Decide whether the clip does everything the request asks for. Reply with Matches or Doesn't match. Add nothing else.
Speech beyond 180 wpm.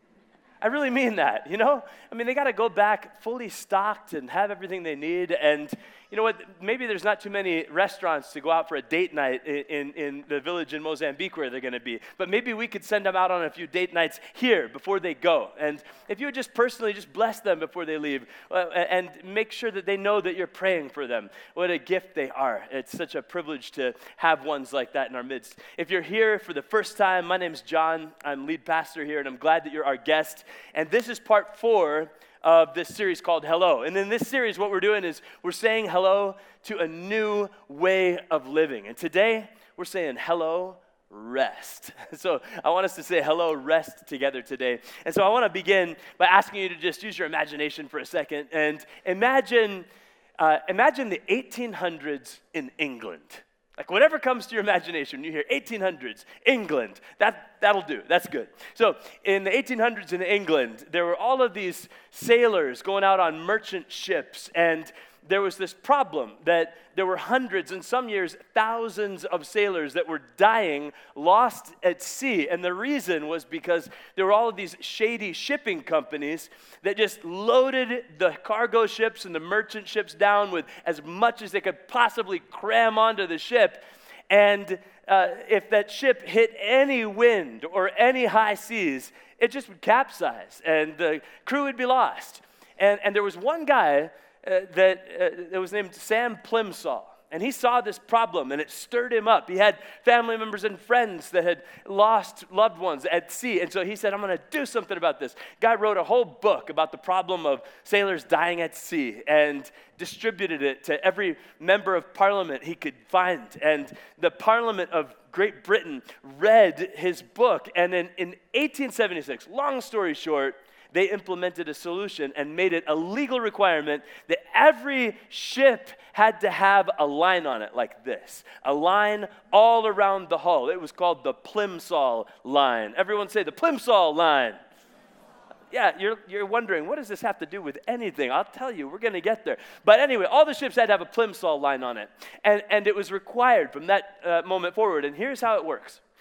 Matches